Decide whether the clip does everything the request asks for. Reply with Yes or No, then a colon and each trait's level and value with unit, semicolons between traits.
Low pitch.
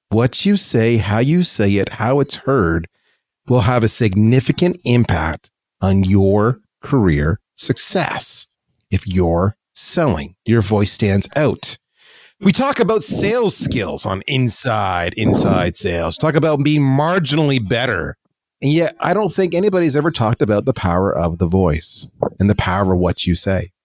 Yes: low, 115 Hz